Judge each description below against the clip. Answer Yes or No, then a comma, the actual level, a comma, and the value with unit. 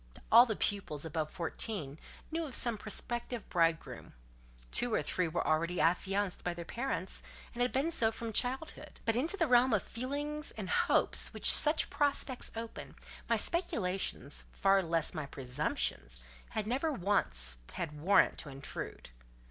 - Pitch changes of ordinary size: No, wide, 7.3 semitones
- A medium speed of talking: Yes, average, 155 wpm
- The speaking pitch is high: Yes, high, 205 Hz